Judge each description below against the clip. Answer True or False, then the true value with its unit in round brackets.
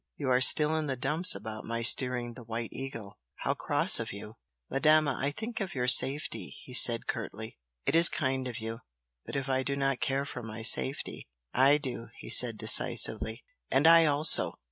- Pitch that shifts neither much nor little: True (3.7 semitones)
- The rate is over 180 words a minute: True (190 wpm)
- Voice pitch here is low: True (130 Hz)